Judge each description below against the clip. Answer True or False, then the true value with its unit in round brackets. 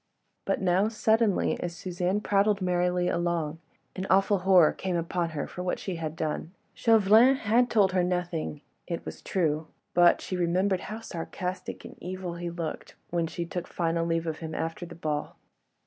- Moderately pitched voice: True (180 Hz)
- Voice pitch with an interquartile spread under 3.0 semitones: True (2.4 semitones)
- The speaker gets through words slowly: False (175 wpm)